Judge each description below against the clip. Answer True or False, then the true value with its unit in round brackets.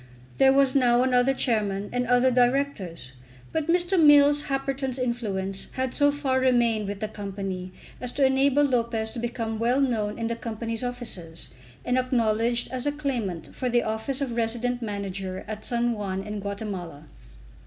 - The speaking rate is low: False (165 wpm)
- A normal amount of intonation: True (3.8 semitones)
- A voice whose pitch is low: False (240 Hz)